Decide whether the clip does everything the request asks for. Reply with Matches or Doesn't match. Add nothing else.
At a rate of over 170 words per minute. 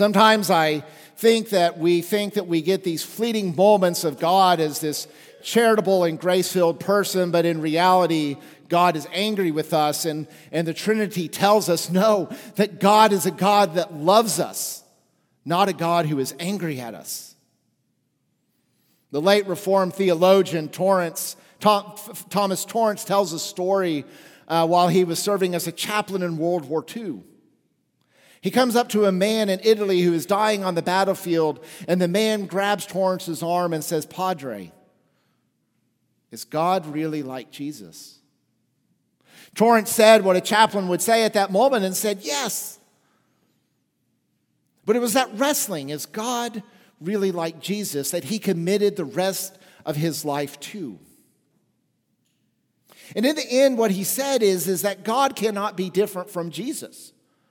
Doesn't match